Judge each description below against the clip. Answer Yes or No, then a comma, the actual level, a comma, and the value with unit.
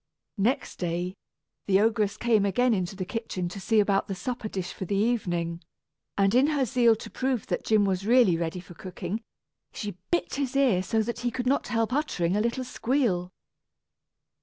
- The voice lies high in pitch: Yes, high, 210 Hz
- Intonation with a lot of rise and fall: No, average, 4.7 semitones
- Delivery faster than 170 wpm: Yes, average, 185 wpm